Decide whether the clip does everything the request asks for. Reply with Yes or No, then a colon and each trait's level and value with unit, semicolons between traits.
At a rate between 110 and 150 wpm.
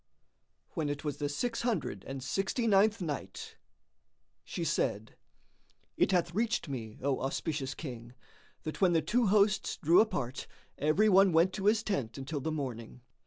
No: average, 160 wpm